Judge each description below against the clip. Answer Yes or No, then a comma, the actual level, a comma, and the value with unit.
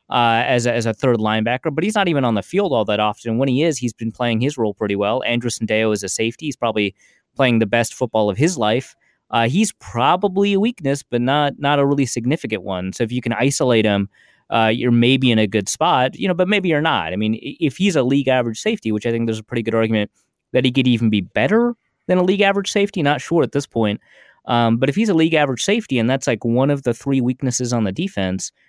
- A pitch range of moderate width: Yes, average, 4.5 semitones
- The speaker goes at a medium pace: No, fast, 255 wpm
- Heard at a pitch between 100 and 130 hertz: Yes, low, 125 Hz